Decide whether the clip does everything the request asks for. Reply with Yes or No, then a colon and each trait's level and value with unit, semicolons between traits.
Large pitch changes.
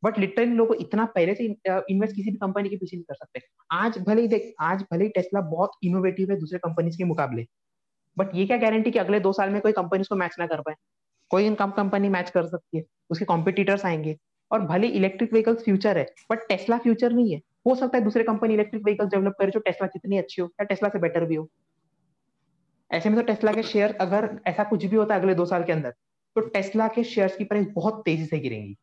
No: average, 3.6 semitones